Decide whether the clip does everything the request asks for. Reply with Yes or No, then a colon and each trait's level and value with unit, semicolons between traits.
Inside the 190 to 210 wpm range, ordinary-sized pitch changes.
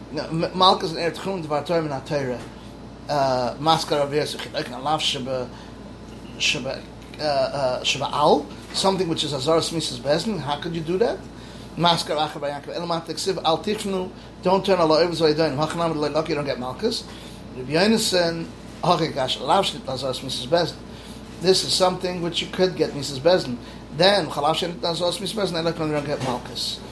No: average, 175 wpm; average, 3.7 semitones